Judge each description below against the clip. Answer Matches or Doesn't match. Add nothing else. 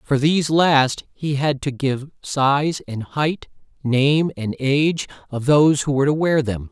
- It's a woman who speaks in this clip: Doesn't match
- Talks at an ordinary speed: Matches